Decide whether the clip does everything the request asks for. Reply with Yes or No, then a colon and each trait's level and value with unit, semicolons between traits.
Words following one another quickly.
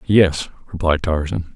No: slow, 115 wpm